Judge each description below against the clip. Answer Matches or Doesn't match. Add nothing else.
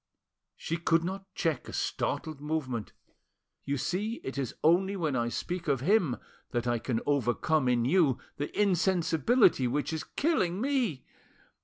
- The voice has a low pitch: Doesn't match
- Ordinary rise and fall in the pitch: Doesn't match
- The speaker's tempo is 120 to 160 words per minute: Matches